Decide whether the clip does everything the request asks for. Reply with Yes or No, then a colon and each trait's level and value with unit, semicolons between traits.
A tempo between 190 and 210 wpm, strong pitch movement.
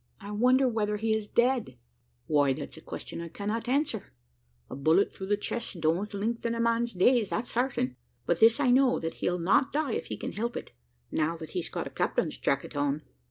Yes: fast, 205 wpm; wide, 5.9 semitones